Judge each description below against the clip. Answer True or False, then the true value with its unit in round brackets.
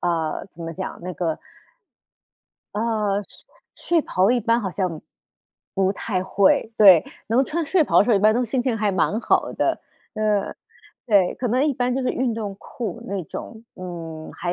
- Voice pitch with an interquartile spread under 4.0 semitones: False (4.6 semitones)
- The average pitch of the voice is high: True (210 Hz)